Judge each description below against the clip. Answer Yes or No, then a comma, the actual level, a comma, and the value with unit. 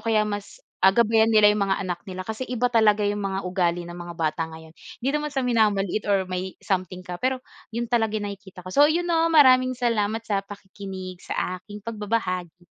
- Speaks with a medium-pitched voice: No, high, 205 Hz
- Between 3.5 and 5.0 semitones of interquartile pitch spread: Yes, average, 3.8 semitones